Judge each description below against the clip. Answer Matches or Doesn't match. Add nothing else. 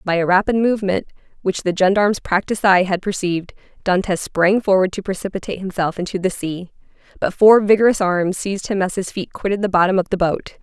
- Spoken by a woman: Matches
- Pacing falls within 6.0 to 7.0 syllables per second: Matches